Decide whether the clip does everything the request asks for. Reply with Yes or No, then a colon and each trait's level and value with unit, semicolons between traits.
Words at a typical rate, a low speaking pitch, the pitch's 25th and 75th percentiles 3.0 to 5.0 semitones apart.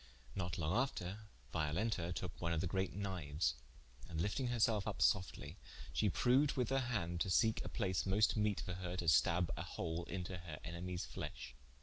Yes: average, 190 wpm; very low, 90 Hz; average, 3.9 semitones